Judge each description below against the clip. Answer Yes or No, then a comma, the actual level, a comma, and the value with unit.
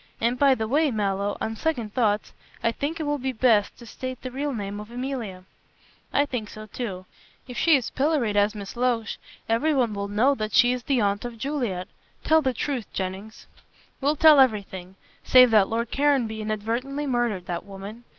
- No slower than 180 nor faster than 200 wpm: Yes, average, 190 wpm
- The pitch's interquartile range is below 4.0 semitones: No, average, 4.3 semitones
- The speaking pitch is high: Yes, high, 235 Hz